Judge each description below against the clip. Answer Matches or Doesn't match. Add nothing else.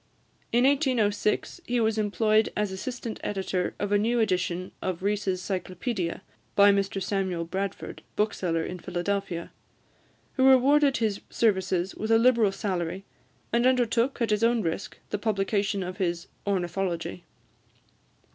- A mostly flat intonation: Doesn't match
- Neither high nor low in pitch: Doesn't match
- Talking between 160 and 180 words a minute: Doesn't match